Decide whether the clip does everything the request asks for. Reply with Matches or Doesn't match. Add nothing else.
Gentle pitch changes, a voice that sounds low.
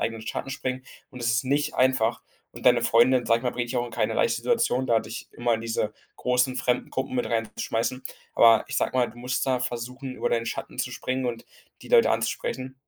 Matches